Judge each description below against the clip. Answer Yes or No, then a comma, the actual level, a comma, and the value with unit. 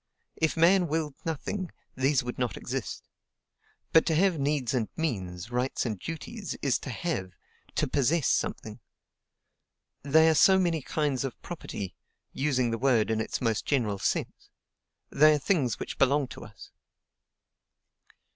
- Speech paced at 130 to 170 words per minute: Yes, average, 145 wpm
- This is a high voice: No, medium, 140 Hz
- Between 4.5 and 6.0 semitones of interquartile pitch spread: Yes, average, 4.9 semitones